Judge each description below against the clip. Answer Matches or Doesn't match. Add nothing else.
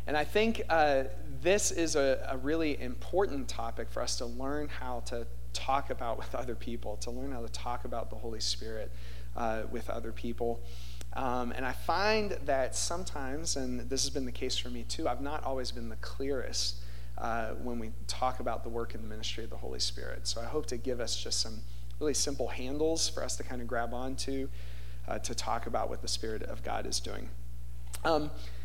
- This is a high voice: Doesn't match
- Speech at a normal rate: Doesn't match